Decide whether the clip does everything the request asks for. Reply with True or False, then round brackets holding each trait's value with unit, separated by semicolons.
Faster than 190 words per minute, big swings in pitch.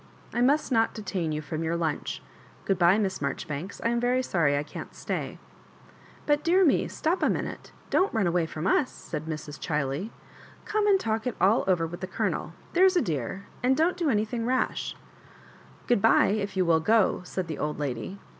True (205 wpm; 7.2 semitones)